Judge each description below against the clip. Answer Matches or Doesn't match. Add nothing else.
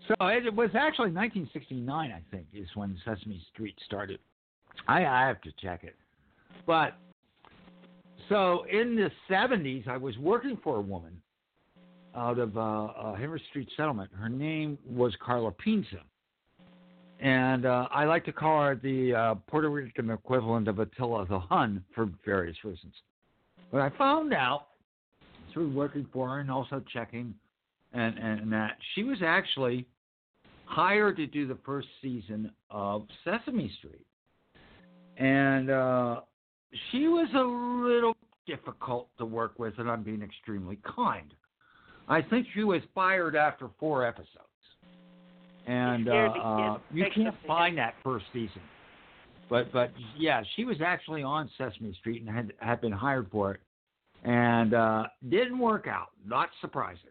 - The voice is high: Doesn't match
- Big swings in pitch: Matches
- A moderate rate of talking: Matches